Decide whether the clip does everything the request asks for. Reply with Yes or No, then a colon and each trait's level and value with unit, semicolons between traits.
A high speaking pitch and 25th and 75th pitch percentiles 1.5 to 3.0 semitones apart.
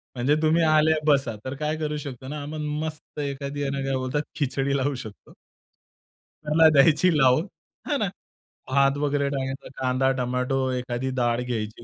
No: medium, 140 Hz; narrow, 2.6 semitones